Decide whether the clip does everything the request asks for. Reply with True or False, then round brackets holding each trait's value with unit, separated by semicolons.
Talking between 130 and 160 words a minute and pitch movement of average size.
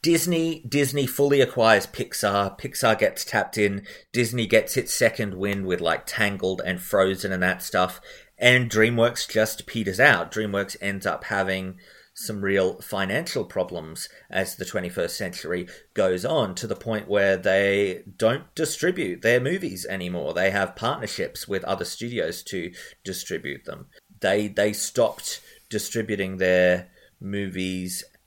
True (140 wpm; 3.2 semitones)